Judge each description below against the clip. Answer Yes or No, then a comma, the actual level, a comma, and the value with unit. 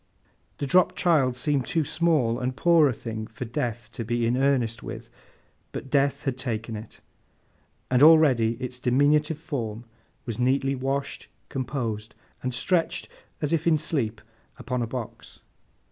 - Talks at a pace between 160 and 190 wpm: No, average, 150 wpm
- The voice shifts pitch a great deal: No, average, 3.6 semitones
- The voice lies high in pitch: No, low, 130 Hz